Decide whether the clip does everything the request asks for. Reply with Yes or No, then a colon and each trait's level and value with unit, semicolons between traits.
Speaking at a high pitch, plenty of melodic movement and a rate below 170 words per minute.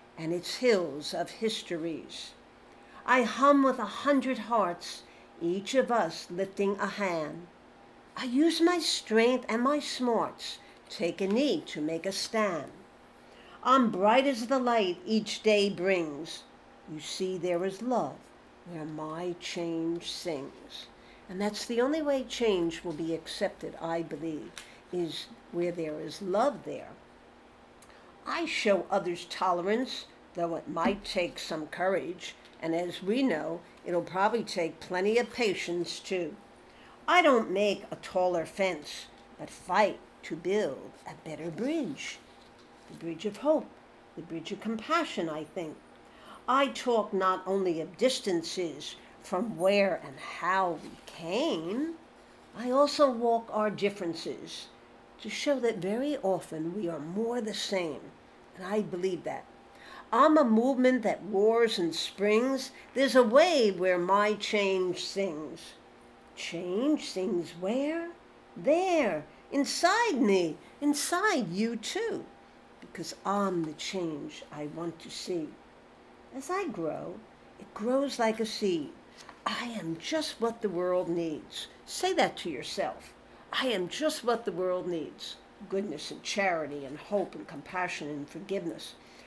Yes: high, 195 Hz; wide, 6.3 semitones; average, 140 wpm